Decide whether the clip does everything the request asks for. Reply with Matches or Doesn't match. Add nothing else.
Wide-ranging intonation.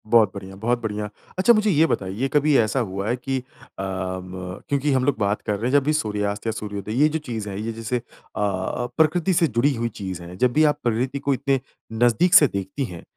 Matches